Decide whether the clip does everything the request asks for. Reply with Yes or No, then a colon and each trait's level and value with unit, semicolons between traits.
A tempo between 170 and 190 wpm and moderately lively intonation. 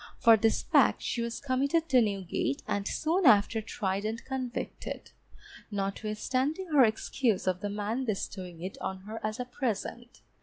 No: average, 155 wpm; average, 4.1 semitones